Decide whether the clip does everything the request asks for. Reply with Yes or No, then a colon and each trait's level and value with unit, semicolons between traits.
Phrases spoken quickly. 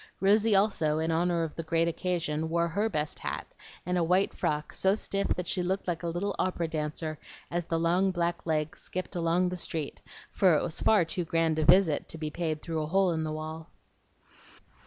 Yes: fast, 210 wpm